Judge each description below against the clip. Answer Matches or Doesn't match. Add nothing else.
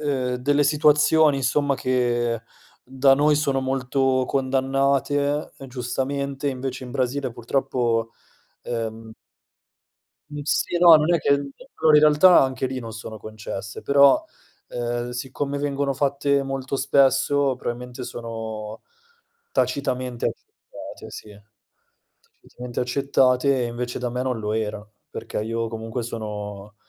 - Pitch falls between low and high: Doesn't match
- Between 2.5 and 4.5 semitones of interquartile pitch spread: Matches